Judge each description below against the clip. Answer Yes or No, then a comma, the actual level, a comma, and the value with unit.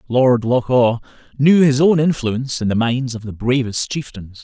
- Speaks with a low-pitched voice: Yes, low, 125 Hz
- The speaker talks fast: No, average, 190 wpm